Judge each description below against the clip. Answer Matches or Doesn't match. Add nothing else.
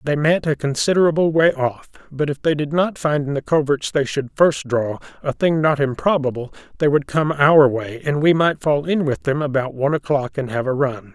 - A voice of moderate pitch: Matches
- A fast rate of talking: Matches